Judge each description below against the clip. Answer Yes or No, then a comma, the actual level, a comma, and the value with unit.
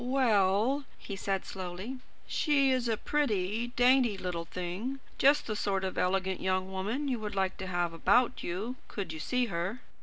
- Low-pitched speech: No, high, 200 Hz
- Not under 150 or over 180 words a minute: Yes, average, 175 wpm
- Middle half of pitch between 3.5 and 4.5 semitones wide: No, average, 5.1 semitones